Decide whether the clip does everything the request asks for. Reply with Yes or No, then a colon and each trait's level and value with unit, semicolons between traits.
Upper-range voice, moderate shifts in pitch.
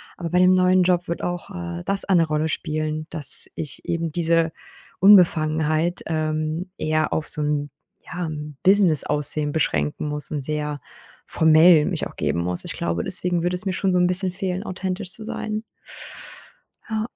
No: medium, 165 Hz; average, 3.1 semitones